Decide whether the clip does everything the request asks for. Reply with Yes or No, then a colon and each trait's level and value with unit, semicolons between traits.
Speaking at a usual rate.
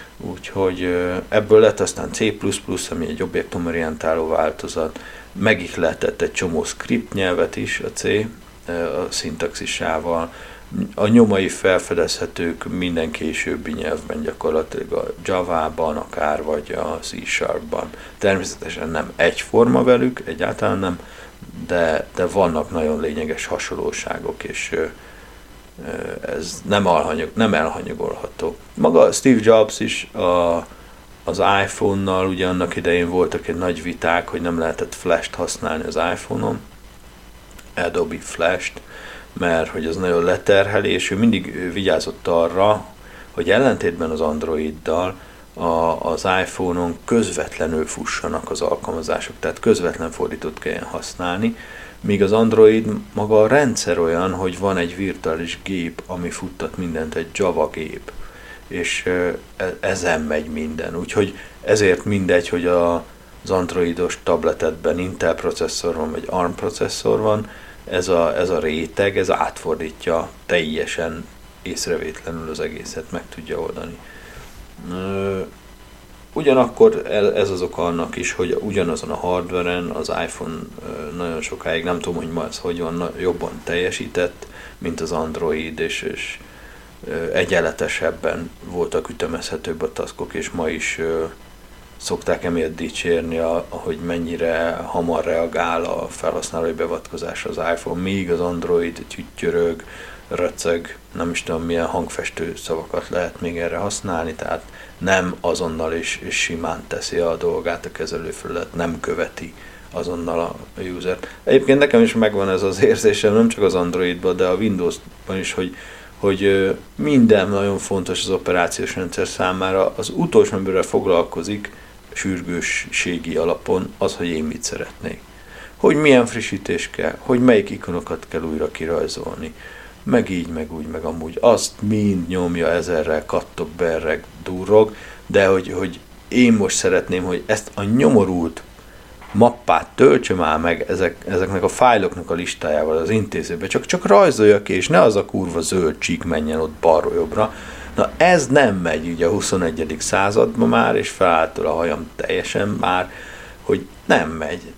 Yes: average, 135 wpm